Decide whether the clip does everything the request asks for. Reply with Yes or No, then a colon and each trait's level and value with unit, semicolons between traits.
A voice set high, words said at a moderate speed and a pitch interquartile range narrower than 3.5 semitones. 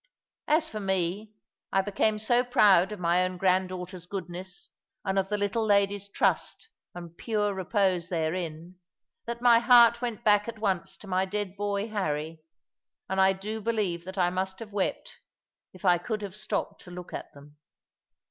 Yes: high, 195 Hz; average, 170 wpm; average, 2.8 semitones